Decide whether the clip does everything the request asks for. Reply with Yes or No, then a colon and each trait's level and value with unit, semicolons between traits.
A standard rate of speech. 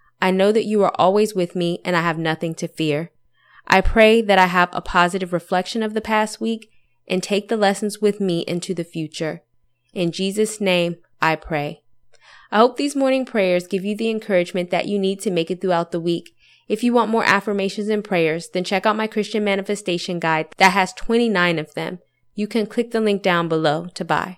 No: fast, 210 wpm